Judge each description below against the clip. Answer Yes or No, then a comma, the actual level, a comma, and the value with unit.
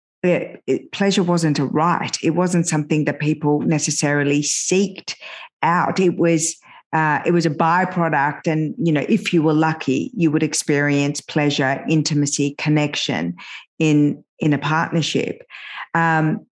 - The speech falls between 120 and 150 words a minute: Yes, average, 140 wpm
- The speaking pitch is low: No, medium, 155 Hz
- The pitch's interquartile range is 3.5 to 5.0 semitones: No, narrow, 2.4 semitones